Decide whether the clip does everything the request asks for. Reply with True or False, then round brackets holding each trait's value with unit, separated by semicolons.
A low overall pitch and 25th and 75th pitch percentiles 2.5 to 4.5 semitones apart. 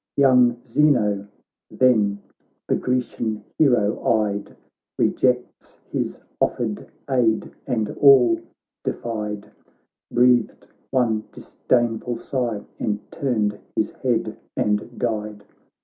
True (115 Hz; 3.1 semitones)